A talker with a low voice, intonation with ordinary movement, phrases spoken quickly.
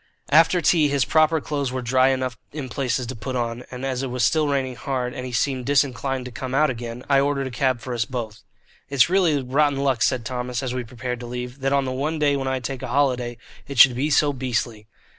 No: low, 130 Hz; narrow, 2.2 semitones; fast, 240 wpm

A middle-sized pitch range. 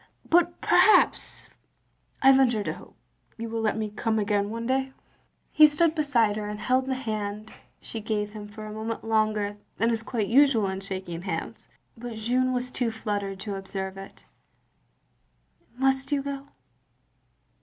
Yes: average, 3.8 semitones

